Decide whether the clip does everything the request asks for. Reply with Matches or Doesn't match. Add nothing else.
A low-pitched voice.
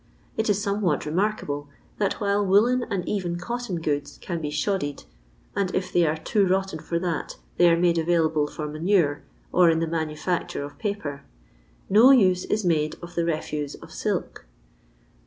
Doesn't match